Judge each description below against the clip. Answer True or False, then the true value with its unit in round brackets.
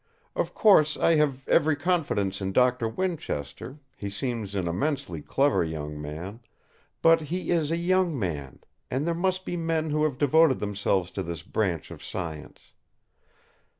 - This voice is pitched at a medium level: False (130 Hz)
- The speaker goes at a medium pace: True (155 wpm)